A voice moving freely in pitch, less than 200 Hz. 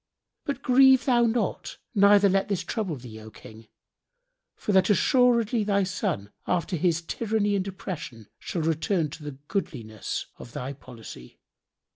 Yes: wide, 7.3 semitones; high, 190 Hz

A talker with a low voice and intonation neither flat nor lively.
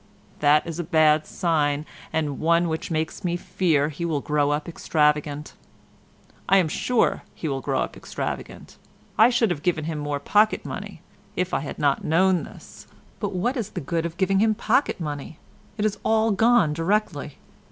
No: medium, 165 Hz; average, 4.2 semitones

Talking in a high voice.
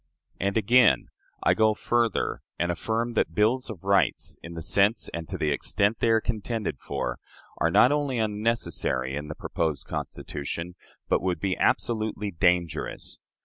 No: low, 100 Hz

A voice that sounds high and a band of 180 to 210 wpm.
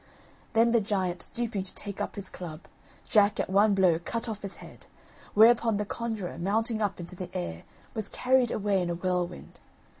Yes: high, 200 Hz; average, 185 wpm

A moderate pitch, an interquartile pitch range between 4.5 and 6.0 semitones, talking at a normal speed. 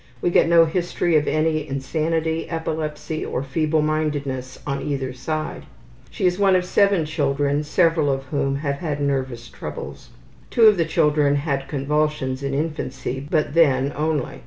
No: medium, 150 Hz; average, 2.8 semitones; average, 155 wpm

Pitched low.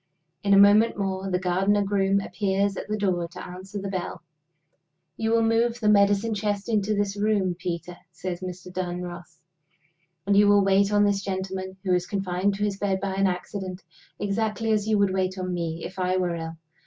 No: high, 195 Hz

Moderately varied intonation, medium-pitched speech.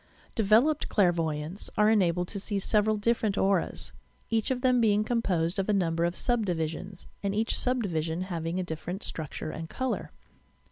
No: average, 4.5 semitones; high, 195 Hz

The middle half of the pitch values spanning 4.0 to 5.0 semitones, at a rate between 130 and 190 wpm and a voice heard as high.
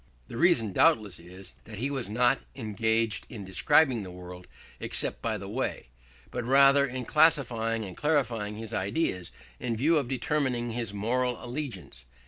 No: average, 4.5 semitones; average, 155 wpm; low, 115 Hz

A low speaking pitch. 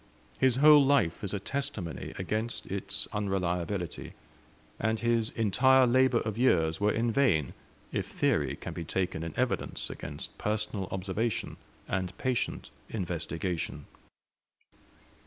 Yes: low, 105 Hz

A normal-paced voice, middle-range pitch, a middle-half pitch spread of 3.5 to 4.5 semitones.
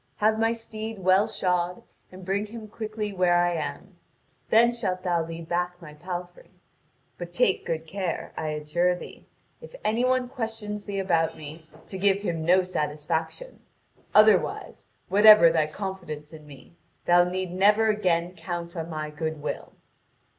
Yes: average, 155 wpm; medium, 180 Hz; average, 4.1 semitones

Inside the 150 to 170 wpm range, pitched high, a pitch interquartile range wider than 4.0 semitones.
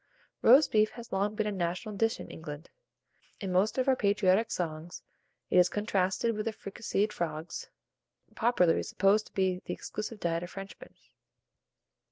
No: average, 160 wpm; high, 195 Hz; average, 3.2 semitones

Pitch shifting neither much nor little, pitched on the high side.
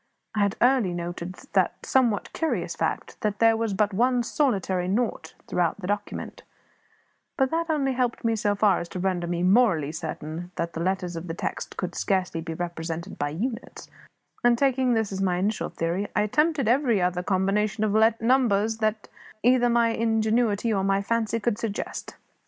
Yes: average, 4.6 semitones; high, 210 Hz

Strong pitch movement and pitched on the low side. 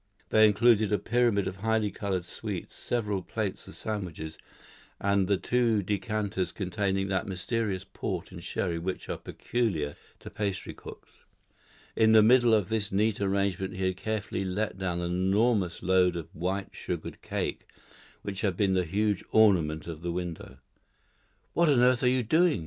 No: average, 3.0 semitones; low, 100 Hz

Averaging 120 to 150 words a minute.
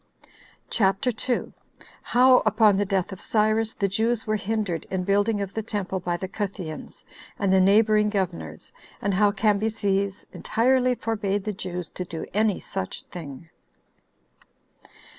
Yes: average, 140 wpm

